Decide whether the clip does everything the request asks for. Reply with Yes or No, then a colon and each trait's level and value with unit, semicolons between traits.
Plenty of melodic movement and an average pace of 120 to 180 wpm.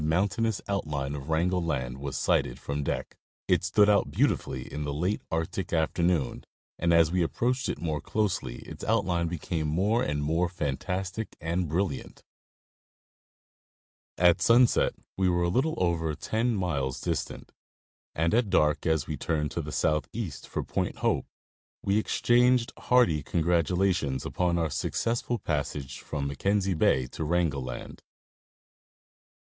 No: average, 4.5 semitones; average, 145 wpm